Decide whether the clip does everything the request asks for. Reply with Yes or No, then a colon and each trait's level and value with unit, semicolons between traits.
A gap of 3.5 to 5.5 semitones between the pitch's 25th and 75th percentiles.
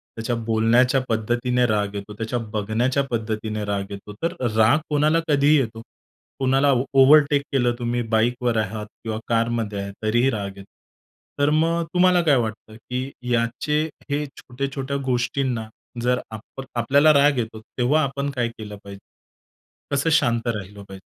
Yes: average, 4.0 semitones